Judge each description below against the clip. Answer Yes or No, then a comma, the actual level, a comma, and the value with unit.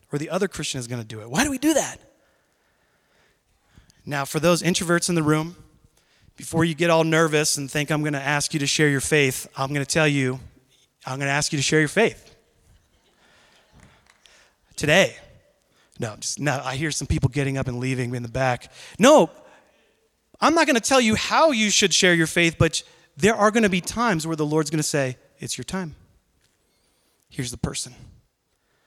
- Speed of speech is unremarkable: Yes, average, 190 wpm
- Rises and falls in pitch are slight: No, average, 4.2 semitones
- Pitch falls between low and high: Yes, medium, 150 Hz